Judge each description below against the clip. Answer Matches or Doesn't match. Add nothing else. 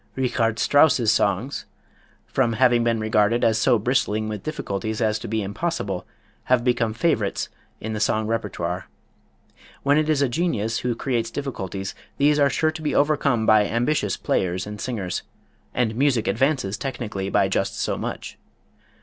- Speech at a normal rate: Matches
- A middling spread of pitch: Matches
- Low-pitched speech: Matches